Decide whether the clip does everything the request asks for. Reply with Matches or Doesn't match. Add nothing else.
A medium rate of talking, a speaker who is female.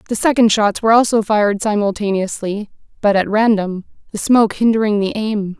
Matches